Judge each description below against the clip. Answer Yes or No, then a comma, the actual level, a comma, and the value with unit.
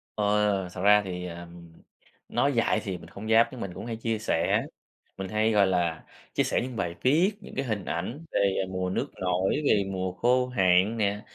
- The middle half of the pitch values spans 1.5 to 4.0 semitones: Yes, average, 3.7 semitones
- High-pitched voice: No, low, 100 Hz